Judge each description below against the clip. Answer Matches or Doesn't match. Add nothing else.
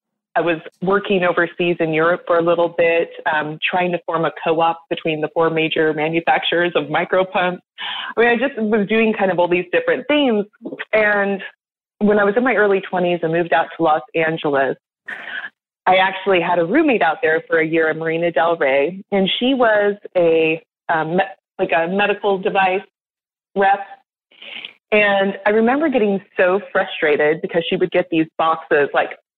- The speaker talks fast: Doesn't match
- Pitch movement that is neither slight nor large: Matches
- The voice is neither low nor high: Matches